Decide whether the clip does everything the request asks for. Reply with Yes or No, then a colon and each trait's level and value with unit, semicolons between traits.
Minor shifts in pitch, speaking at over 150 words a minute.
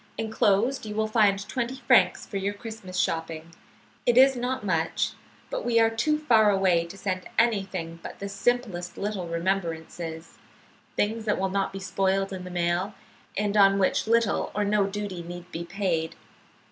No: average, 3.5 semitones; average, 170 wpm